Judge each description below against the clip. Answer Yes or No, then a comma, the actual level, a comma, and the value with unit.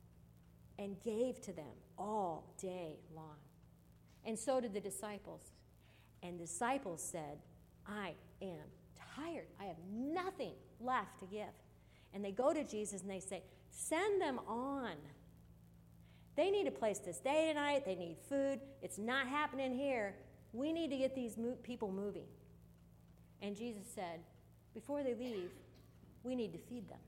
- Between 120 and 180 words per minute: Yes, average, 150 wpm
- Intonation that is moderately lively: No, wide, 7.0 semitones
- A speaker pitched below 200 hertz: No, high, 210 Hz